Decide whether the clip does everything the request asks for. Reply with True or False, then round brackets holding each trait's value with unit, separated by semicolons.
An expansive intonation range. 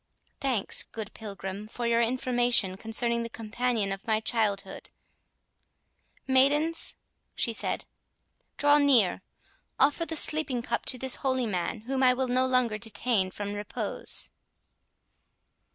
False (3.5 semitones)